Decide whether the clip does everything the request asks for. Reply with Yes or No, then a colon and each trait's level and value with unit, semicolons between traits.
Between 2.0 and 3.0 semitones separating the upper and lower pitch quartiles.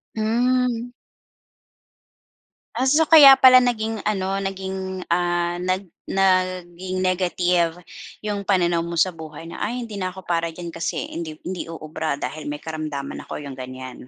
No: average, 3.5 semitones